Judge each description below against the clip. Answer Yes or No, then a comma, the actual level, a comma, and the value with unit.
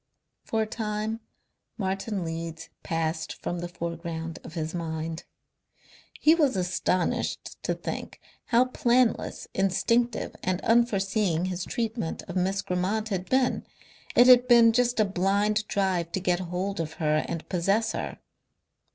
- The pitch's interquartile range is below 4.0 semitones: No, average, 4.7 semitones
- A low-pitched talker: No, high, 190 Hz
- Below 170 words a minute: Yes, average, 140 wpm